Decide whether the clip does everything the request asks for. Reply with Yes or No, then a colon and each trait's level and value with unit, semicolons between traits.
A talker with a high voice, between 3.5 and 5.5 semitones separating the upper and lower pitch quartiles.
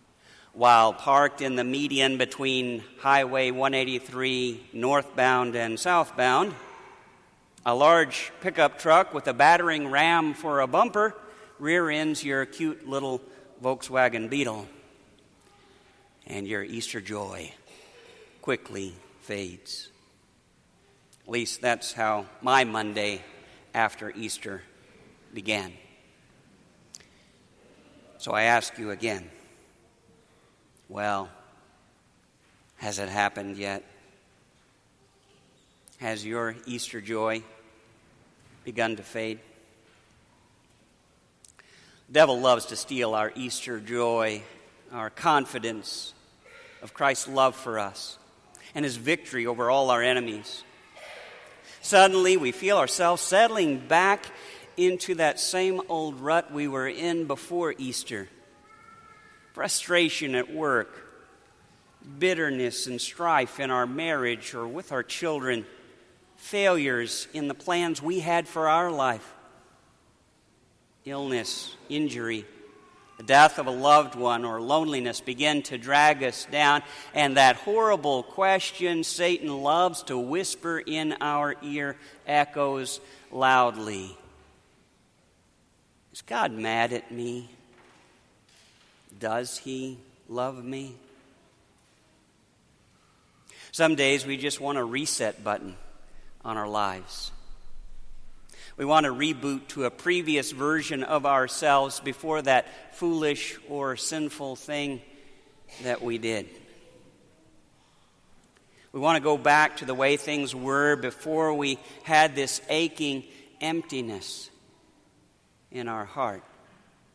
No: low, 135 Hz; average, 4.3 semitones